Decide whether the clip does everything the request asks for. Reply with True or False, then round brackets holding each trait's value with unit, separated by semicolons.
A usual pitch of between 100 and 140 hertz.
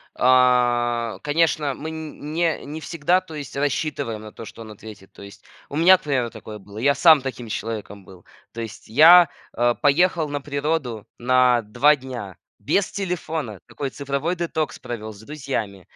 True (135 Hz)